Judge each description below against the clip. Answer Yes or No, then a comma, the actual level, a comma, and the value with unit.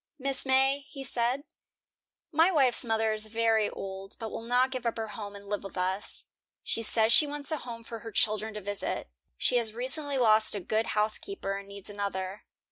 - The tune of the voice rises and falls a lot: No, average, 3.8 semitones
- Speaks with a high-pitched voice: Yes, high, 225 Hz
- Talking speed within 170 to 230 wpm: Yes, average, 200 wpm